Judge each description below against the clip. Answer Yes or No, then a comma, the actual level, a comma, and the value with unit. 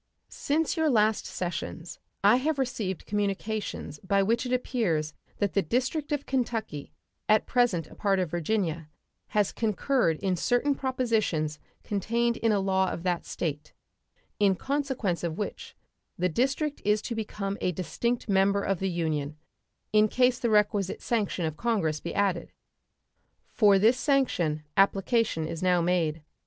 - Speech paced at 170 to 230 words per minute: No, average, 150 wpm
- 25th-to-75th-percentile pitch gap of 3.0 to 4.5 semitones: No, average, 5.2 semitones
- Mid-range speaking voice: No, high, 200 Hz